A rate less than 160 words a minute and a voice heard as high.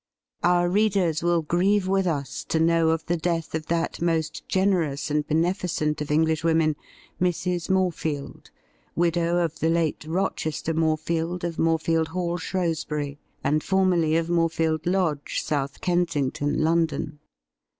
No: slow, 135 wpm; medium, 165 Hz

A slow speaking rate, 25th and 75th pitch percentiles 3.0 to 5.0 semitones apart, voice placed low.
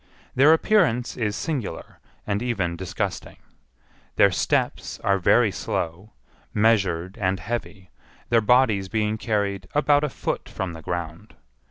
Yes: slow, 130 wpm; average, 4.2 semitones; low, 105 Hz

